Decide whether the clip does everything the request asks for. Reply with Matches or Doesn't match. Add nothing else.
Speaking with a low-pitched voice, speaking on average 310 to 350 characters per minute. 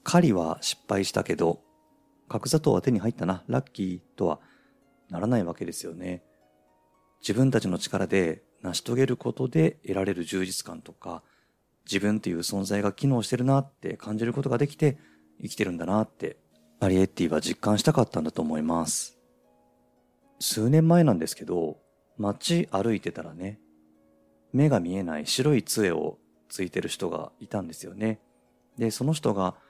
Matches